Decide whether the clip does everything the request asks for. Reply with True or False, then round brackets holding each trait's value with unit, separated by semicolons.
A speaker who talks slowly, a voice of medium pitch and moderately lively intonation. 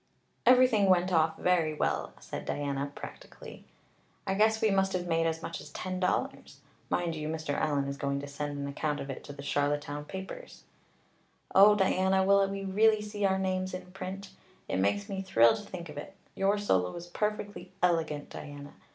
False (185 wpm; 180 Hz; 5.0 semitones)